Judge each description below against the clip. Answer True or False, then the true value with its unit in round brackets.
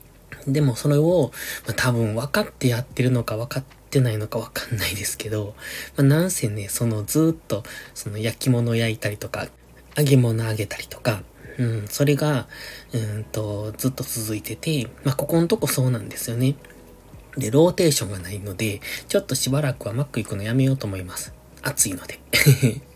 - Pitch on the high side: False (120 Hz)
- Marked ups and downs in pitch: False (4.3 semitones)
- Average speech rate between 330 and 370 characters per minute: True (365 characters per minute)